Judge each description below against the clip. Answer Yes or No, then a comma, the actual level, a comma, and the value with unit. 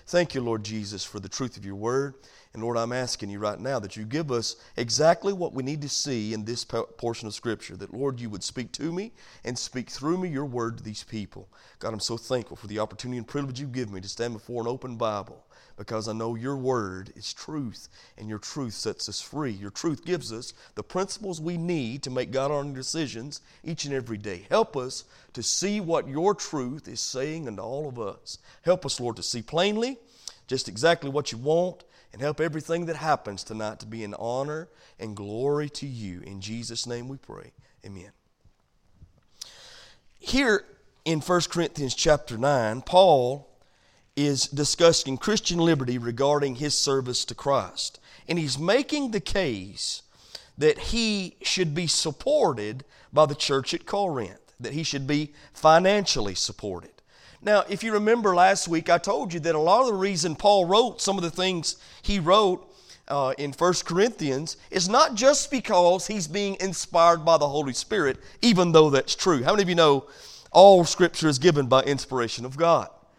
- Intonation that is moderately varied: No, wide, 6.5 semitones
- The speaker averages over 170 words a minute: Yes, average, 190 wpm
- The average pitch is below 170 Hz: Yes, medium, 140 Hz